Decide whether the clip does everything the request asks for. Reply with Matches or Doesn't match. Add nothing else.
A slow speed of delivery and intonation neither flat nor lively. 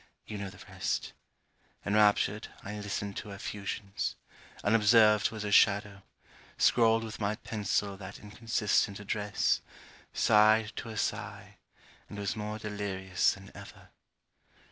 Doesn't match